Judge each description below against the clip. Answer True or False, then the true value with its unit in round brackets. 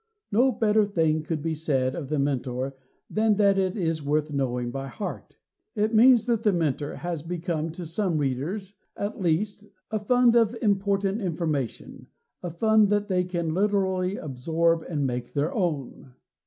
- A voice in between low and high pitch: True (175 Hz)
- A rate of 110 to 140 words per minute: False (165 wpm)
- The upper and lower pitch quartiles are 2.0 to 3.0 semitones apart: False (5.4 semitones)